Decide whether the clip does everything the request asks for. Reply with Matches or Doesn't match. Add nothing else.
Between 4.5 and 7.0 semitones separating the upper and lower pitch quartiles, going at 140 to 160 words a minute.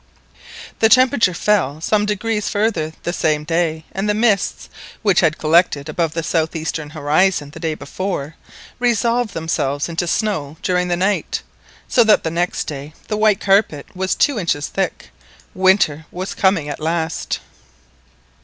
Matches